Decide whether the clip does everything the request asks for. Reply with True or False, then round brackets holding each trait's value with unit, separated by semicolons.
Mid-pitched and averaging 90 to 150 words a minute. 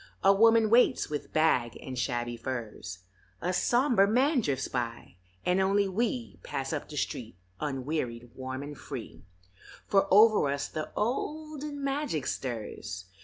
True (155 Hz; 140 wpm)